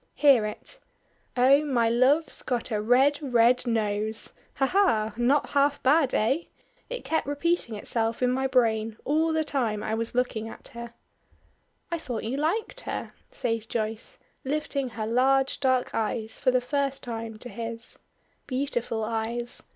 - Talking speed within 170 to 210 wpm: No, average, 155 wpm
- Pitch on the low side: No, high, 245 Hz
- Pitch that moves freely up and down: No, average, 3.8 semitones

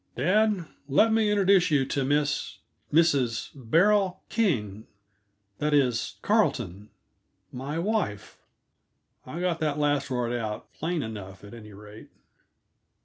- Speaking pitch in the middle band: Yes, medium, 145 Hz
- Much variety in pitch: Yes, wide, 7.8 semitones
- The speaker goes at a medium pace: No, slow, 120 wpm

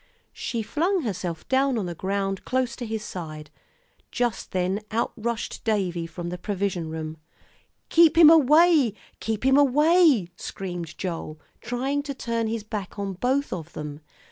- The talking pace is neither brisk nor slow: Yes, average, 155 wpm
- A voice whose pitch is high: Yes, high, 215 Hz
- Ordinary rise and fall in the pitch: No, wide, 6.8 semitones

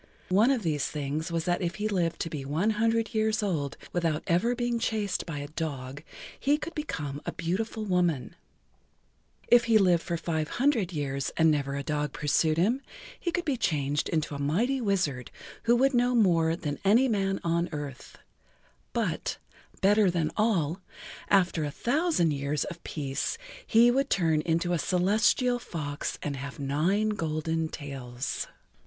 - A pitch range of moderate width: No, wide, 6.6 semitones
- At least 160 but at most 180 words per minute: Yes, average, 170 wpm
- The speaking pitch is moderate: Yes, medium, 170 Hz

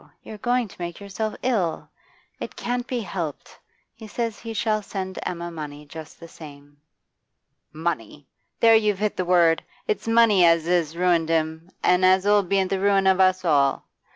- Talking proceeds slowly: No, average, 175 wpm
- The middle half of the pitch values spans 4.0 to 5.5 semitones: Yes, average, 4.3 semitones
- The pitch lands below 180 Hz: No, medium, 185 Hz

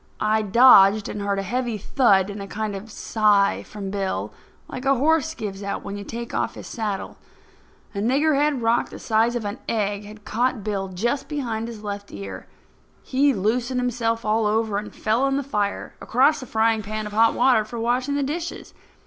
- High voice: Yes, high, 220 Hz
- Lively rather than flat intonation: No, average, 3.5 semitones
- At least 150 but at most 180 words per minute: No, average, 200 wpm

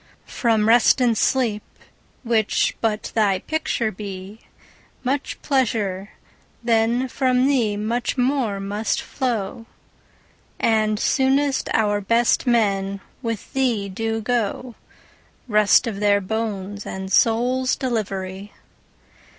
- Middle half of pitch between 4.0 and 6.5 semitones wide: No, average, 3.2 semitones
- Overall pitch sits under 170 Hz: No, high, 225 Hz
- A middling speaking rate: No, slow, 110 wpm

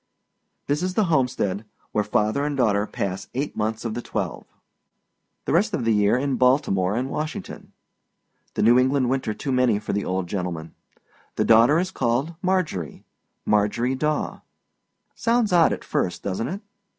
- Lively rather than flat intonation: Yes, wide, 6.2 semitones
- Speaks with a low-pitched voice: Yes, low, 125 Hz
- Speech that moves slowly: No, average, 160 wpm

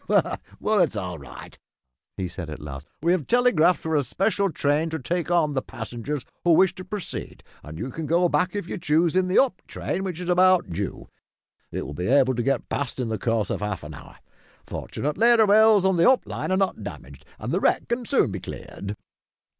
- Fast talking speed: Yes, fast, 215 wpm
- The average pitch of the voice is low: No, medium, 160 Hz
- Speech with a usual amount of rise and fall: No, wide, 7.6 semitones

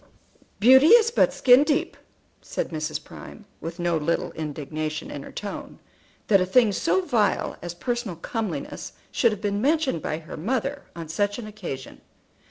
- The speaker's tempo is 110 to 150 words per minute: No, average, 165 wpm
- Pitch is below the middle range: No, high, 205 Hz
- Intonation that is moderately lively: No, wide, 7.4 semitones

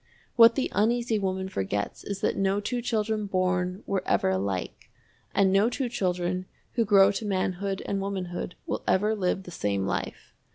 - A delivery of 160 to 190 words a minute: Yes, average, 170 wpm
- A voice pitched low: No, high, 195 Hz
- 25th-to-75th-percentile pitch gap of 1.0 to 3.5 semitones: Yes, average, 2.7 semitones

